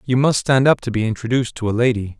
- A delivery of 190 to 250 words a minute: No, fast, 275 wpm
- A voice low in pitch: Yes, low, 120 Hz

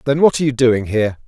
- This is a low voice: Yes, low, 125 Hz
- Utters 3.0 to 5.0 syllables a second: No, 7.3 syllables/s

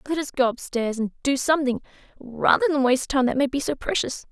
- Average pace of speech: No, fast, 235 wpm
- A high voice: Yes, very high, 265 Hz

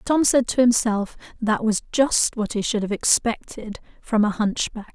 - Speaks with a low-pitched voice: No, high, 225 Hz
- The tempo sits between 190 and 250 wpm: Yes, average, 195 wpm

